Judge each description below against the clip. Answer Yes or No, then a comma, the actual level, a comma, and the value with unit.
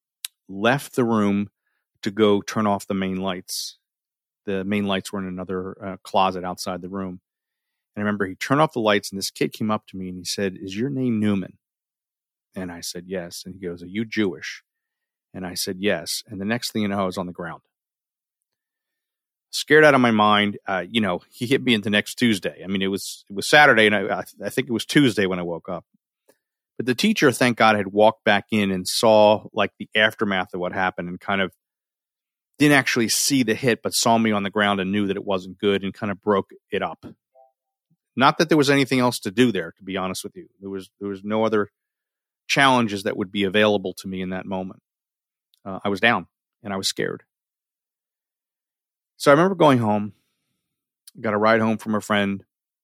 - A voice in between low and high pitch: No, low, 105 Hz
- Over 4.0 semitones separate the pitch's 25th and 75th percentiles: No, average, 3.4 semitones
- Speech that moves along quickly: Yes, fast, 220 wpm